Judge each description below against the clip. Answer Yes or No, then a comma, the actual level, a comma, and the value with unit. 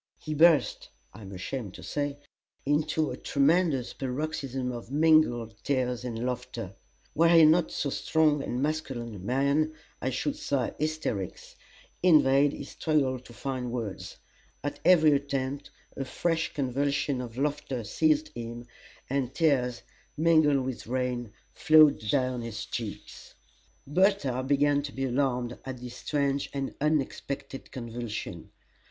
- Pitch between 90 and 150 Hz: Yes, low, 135 Hz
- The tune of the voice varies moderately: Yes, average, 3.5 semitones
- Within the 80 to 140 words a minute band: Yes, slow, 135 wpm